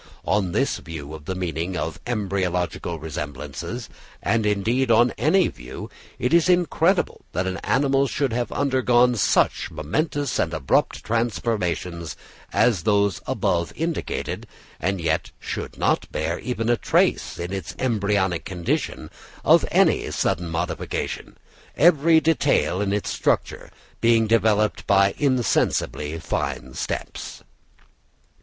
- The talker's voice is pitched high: No, low, 105 Hz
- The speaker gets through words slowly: Yes, slow, 125 wpm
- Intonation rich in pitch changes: Yes, wide, 6.5 semitones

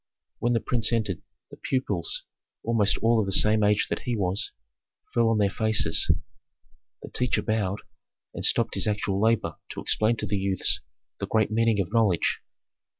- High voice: No, low, 110 Hz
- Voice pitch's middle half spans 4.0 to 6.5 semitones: No, narrow, 2.5 semitones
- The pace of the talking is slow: No, average, 170 wpm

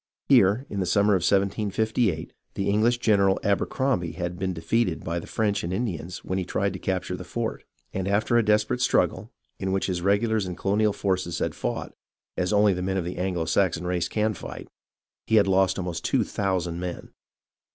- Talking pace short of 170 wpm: No, average, 195 wpm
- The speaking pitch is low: Yes, very low, 95 Hz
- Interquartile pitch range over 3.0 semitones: No, average, 2.7 semitones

